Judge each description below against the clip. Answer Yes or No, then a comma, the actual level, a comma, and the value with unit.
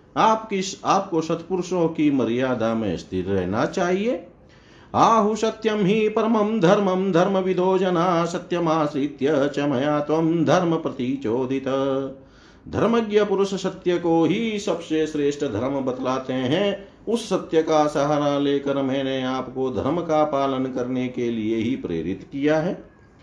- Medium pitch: Yes, medium, 155 Hz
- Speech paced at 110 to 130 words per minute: Yes, average, 125 wpm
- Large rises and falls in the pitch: Yes, wide, 5.7 semitones